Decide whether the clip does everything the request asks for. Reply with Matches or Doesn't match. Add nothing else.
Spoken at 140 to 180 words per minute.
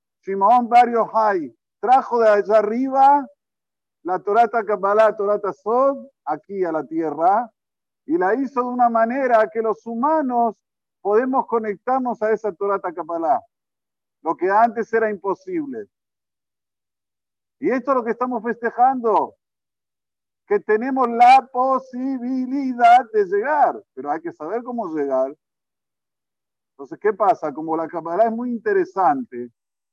Doesn't match